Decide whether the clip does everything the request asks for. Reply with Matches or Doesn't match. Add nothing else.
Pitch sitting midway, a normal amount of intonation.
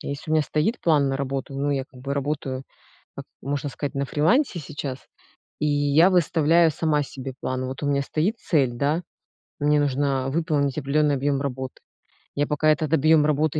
Doesn't match